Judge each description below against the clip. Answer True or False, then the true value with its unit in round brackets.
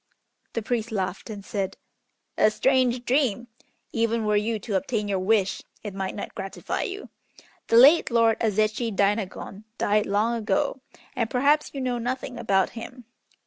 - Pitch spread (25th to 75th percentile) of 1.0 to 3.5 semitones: True (3.1 semitones)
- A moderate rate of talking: True (155 wpm)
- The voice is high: True (225 Hz)